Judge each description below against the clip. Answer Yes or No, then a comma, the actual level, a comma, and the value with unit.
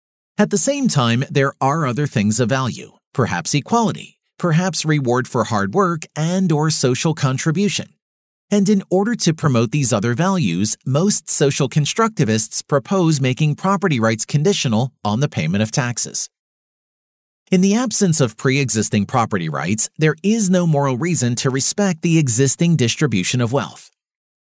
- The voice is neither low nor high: Yes, medium, 150 Hz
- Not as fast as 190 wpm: Yes, average, 150 wpm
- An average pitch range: No, wide, 6.4 semitones